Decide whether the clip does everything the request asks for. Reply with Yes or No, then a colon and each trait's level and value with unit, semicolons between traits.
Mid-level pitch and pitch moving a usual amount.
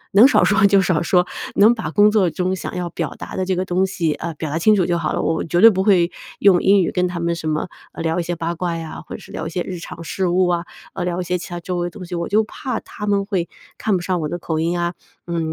No: medium, 180 Hz; narrow, 2.0 semitones